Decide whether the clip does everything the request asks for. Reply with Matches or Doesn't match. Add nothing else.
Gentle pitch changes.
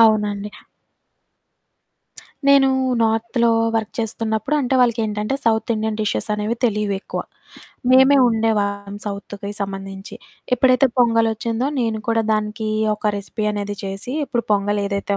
Matches